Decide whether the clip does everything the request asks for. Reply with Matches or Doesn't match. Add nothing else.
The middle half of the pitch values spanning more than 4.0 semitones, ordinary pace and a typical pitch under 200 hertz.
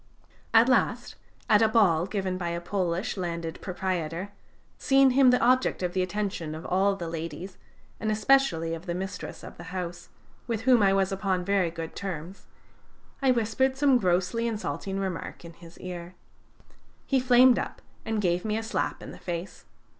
Matches